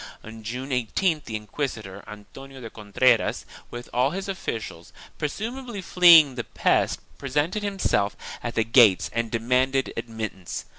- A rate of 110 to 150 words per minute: Yes, average, 140 wpm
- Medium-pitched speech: No, low, 125 Hz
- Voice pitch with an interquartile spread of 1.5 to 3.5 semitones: No, average, 5.2 semitones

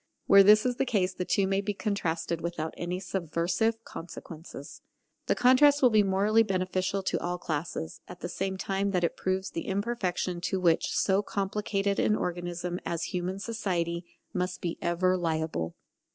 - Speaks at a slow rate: No, average, 165 wpm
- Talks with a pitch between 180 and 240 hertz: Yes, medium, 185 Hz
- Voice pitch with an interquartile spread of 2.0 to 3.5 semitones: Yes, narrow, 2.6 semitones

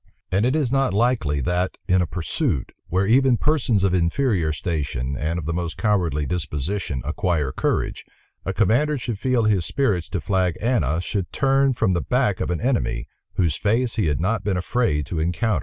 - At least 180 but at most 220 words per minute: Yes, average, 190 wpm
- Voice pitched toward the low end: Yes, very low, 95 Hz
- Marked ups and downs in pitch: Yes, wide, 6.2 semitones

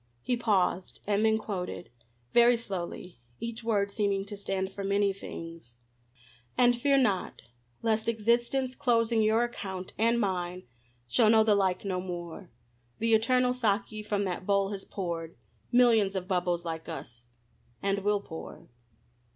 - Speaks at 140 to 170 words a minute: Yes, average, 145 wpm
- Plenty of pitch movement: No, average, 3.8 semitones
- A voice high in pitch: Yes, high, 200 Hz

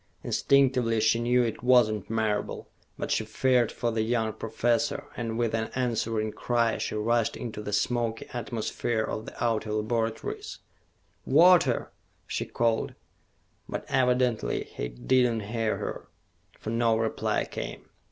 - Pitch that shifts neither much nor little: No, narrow, 1.7 semitones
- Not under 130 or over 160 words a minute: Yes, average, 140 wpm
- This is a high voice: No, low, 115 Hz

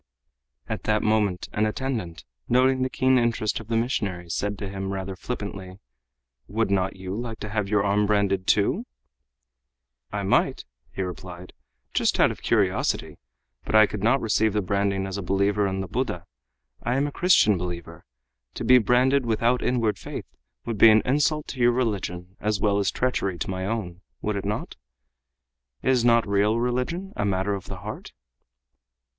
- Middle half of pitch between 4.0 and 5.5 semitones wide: No, average, 3.6 semitones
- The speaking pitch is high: No, low, 105 Hz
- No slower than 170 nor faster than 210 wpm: Yes, average, 175 wpm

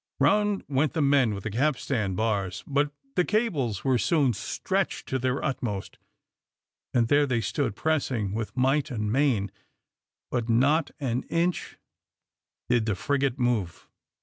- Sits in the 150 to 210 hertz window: No, low, 130 Hz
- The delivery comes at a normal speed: Yes, average, 145 wpm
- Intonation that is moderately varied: Yes, average, 4.5 semitones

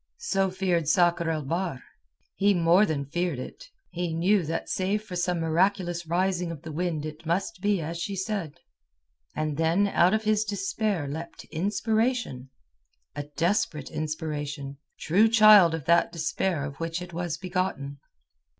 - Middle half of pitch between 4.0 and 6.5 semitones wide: No, average, 3.6 semitones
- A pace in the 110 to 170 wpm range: Yes, average, 150 wpm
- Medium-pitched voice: Yes, medium, 175 Hz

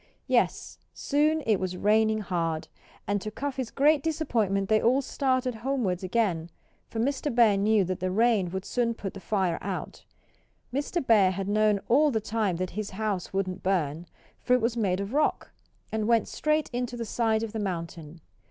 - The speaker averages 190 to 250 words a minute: No, average, 180 wpm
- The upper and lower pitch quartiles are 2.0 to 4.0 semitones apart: No, average, 4.4 semitones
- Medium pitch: No, high, 215 Hz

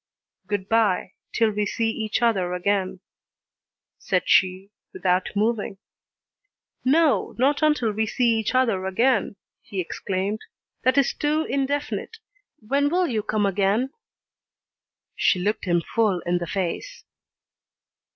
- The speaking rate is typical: No, slow, 125 wpm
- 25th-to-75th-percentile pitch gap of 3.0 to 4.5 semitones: No, average, 5.0 semitones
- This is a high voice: Yes, high, 215 Hz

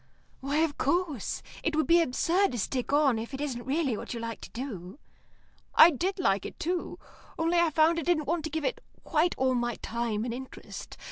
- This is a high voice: Yes, very high, 285 Hz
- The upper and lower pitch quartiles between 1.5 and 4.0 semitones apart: No, wide, 5.5 semitones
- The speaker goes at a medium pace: No, fast, 210 wpm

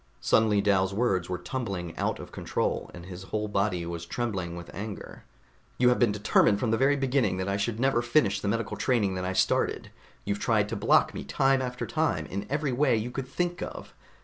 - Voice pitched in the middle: No, low, 105 Hz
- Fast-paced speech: Yes, fast, 210 wpm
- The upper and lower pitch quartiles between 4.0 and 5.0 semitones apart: Yes, average, 4.7 semitones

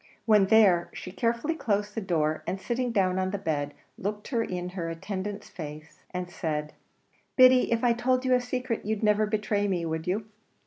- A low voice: No, high, 205 Hz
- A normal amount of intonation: Yes, average, 4.4 semitones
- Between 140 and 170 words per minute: No, average, 185 wpm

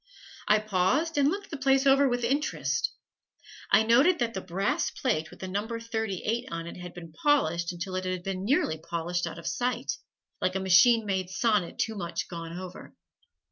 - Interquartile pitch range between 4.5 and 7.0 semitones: Yes, wide, 5.6 semitones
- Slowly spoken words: No, average, 185 wpm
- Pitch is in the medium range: No, high, 195 Hz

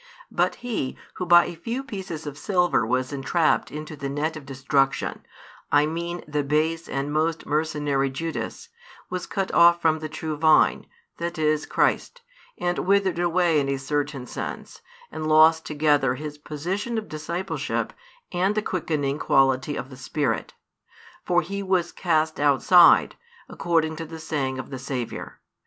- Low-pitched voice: No, medium, 155 Hz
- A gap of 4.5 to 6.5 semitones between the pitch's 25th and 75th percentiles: No, average, 3.1 semitones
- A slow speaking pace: No, average, 155 wpm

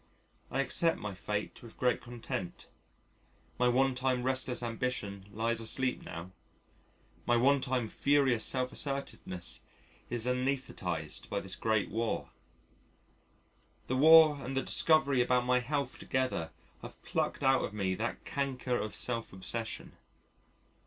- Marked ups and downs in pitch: No, average, 3.1 semitones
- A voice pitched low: Yes, low, 125 Hz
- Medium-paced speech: No, slow, 130 wpm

